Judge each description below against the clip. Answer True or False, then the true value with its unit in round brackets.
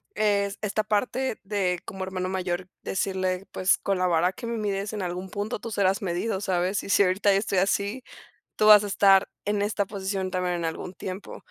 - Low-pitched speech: False (195 Hz)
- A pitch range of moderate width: False (2.0 semitones)